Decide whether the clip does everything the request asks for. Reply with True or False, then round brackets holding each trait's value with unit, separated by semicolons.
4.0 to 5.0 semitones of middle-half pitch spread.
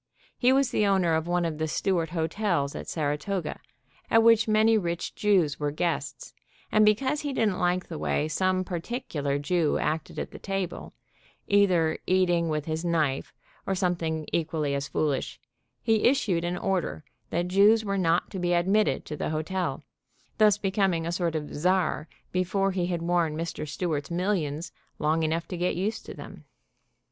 False (3.6 semitones)